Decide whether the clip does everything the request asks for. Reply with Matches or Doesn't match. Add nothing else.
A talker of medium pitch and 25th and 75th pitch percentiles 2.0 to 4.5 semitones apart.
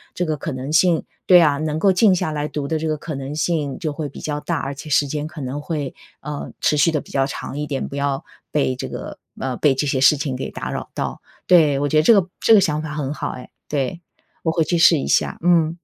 Matches